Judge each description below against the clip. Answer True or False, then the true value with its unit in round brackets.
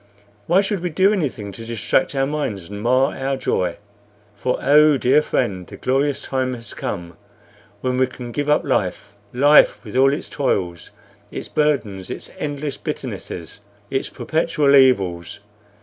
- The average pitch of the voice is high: False (130 Hz)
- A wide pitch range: True (5.7 semitones)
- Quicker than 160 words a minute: False (155 wpm)